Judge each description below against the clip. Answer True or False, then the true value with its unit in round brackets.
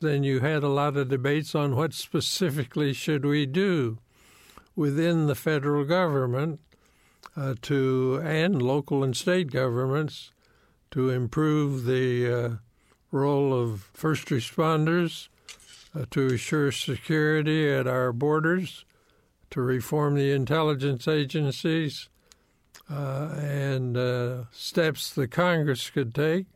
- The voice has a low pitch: False (145 Hz)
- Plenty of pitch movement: False (3.2 semitones)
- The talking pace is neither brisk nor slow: False (120 wpm)